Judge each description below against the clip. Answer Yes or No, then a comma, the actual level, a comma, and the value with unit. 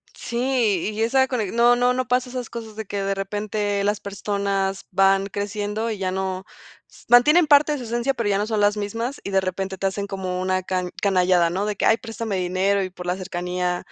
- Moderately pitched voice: No, high, 200 Hz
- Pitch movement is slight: No, average, 3.2 semitones